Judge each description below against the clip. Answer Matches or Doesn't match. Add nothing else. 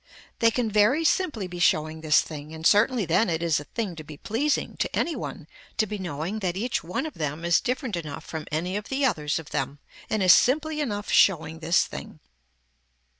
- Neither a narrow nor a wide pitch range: Doesn't match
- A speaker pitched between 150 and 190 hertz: Matches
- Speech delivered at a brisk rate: Matches